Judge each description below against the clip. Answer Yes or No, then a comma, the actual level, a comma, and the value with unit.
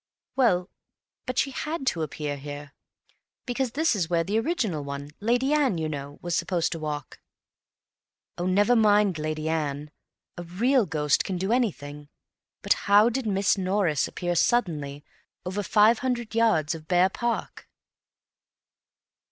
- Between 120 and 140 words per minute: Yes, slow, 135 wpm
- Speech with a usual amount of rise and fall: No, wide, 6.8 semitones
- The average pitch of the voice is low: No, medium, 185 Hz